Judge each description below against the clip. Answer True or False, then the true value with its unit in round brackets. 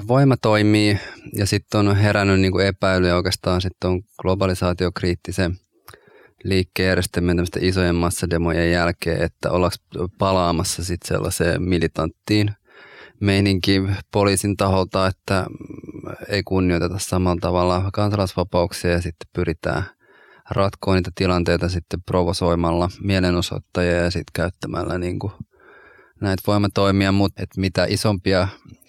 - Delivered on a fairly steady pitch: True (2.1 semitones)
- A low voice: True (95 Hz)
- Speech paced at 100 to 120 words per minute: True (105 wpm)